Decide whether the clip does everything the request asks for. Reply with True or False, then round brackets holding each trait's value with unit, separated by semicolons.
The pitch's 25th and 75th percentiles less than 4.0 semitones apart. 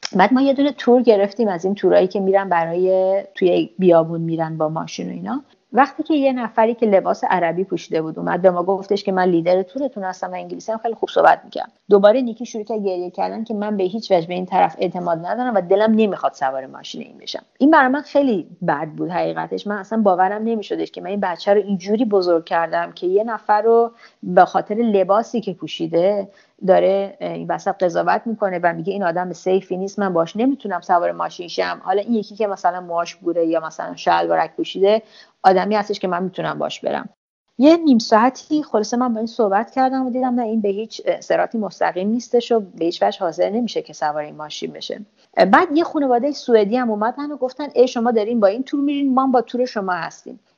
False (4.6 semitones)